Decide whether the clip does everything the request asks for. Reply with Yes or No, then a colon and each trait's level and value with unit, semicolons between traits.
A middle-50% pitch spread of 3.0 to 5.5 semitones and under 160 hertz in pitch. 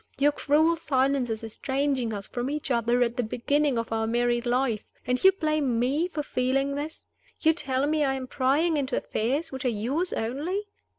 No: average, 3.5 semitones; very high, 265 Hz